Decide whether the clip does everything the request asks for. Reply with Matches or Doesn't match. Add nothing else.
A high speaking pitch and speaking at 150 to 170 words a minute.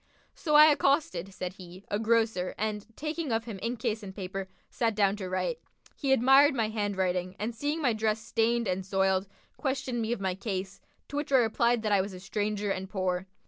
Doesn't match